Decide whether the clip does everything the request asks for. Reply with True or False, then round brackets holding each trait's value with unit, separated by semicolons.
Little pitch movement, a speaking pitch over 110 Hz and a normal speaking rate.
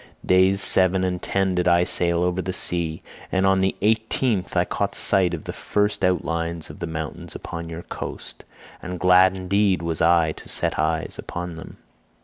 False (2.1 semitones; 90 Hz; 175 wpm)